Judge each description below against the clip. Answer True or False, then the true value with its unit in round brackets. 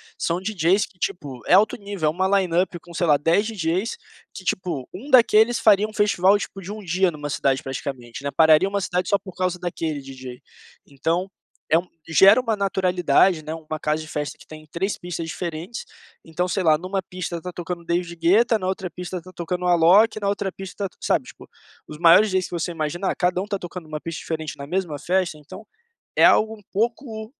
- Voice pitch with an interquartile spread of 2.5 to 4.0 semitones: True (3.4 semitones)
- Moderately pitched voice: True (180 Hz)